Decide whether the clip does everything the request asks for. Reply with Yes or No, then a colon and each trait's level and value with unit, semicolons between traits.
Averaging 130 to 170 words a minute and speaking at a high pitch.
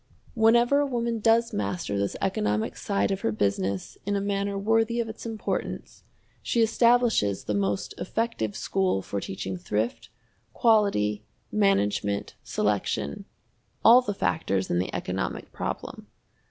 Yes: slow, 135 wpm; high, 195 Hz